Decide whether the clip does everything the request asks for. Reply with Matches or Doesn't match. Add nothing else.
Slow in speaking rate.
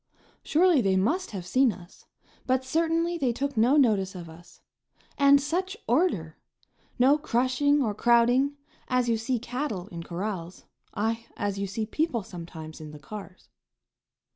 Doesn't match